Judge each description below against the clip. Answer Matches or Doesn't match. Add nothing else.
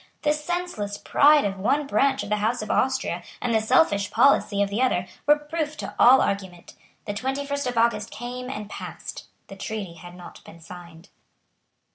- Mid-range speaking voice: Doesn't match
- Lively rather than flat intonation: Matches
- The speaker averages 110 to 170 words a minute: Doesn't match